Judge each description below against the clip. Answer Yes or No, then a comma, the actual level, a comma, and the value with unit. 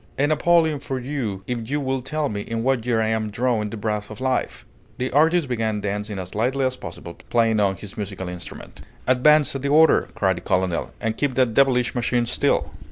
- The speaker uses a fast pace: Yes, fast, 210 wpm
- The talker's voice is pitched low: Yes, low, 120 Hz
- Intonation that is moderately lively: Yes, average, 4.3 semitones